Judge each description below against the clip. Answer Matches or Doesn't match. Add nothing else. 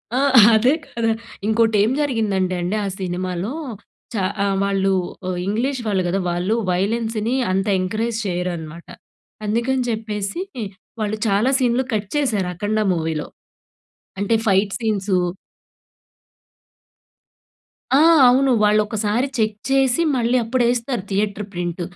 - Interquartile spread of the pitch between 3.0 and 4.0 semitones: Matches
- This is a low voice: Doesn't match